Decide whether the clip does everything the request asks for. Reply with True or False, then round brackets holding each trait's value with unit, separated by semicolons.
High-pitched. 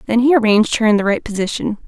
True (220 Hz)